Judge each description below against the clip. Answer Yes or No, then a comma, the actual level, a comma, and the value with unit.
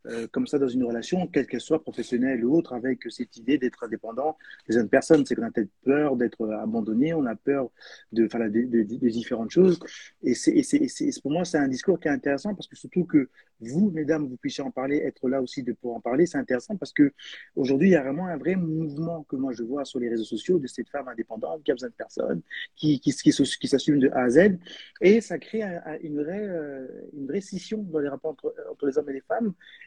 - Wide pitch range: Yes, wide, 6.0 semitones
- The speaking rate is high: Yes, fast, 255 wpm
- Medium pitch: Yes, medium, 145 Hz